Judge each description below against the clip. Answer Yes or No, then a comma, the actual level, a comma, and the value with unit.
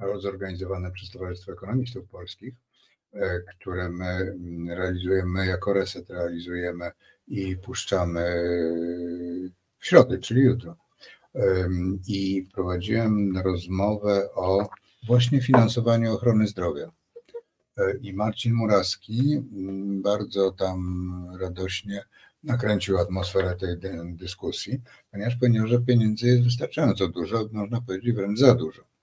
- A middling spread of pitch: Yes, average, 4.0 semitones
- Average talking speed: No, slow, 95 wpm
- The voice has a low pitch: Yes, very low, 95 Hz